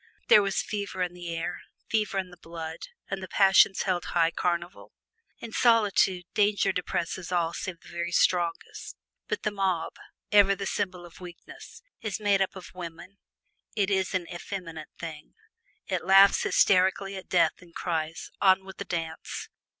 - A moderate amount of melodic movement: No, narrow, 2.3 semitones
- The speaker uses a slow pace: No, average, 165 wpm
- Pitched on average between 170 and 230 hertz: Yes, medium, 185 Hz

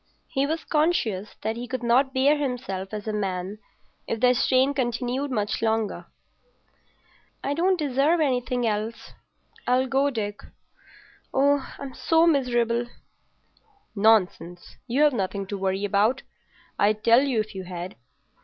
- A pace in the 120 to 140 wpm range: Yes, slow, 135 wpm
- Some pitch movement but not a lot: Yes, average, 4.6 semitones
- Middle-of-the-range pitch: No, high, 240 Hz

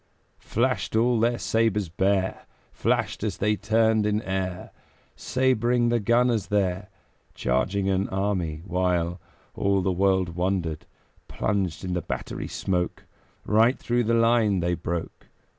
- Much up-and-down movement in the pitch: No, average, 3.7 semitones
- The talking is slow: Yes, slow, 130 wpm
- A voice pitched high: No, low, 100 Hz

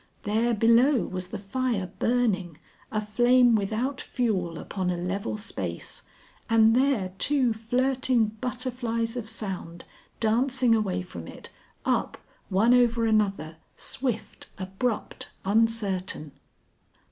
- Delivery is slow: Yes, slow, 110 wpm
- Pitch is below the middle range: No, high, 225 Hz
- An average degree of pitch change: Yes, average, 4.1 semitones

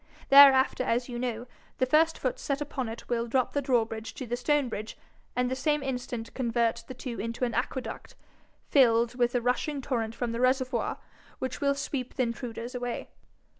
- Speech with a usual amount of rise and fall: No, narrow, 2.2 semitones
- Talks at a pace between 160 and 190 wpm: Yes, average, 185 wpm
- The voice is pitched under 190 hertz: No, very high, 250 Hz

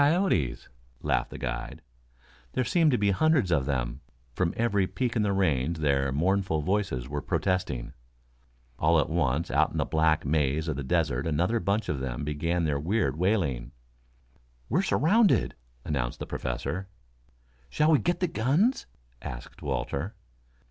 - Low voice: Yes, very low, 85 Hz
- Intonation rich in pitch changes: Yes, wide, 7.0 semitones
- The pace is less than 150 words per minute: No, average, 155 wpm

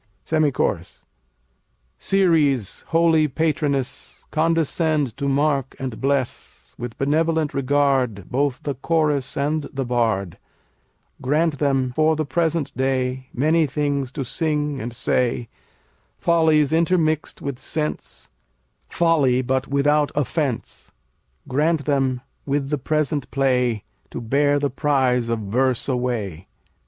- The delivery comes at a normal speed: No, slow, 115 wpm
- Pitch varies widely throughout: No, average, 3.3 semitones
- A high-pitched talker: No, medium, 140 Hz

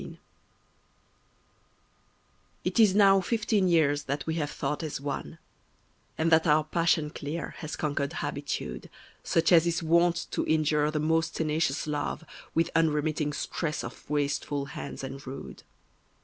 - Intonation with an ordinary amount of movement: No, narrow, 2.2 semitones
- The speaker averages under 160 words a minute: Yes, average, 140 wpm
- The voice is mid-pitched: Yes, medium, 155 Hz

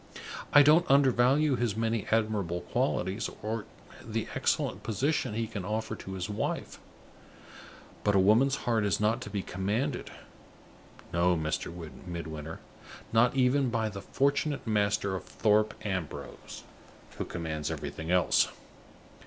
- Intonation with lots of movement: No, average, 4.4 semitones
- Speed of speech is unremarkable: No, slow, 130 wpm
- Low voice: Yes, low, 110 Hz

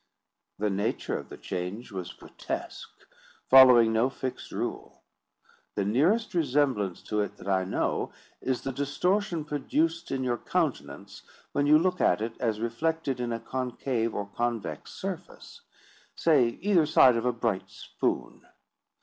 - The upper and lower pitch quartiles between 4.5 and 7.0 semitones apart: Yes, average, 5.3 semitones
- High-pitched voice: No, low, 125 Hz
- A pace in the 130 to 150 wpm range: Yes, average, 140 wpm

